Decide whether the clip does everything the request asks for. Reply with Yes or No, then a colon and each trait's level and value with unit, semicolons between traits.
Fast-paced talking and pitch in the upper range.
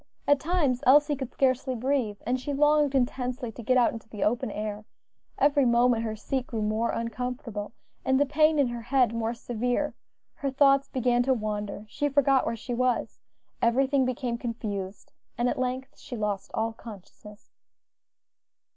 No: average, 165 wpm; high, 245 Hz